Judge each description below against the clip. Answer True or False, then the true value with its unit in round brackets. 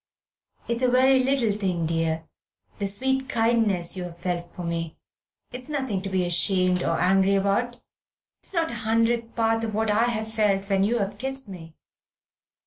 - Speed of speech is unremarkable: True (170 wpm)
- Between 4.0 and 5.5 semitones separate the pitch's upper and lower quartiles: True (4.6 semitones)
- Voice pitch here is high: True (210 Hz)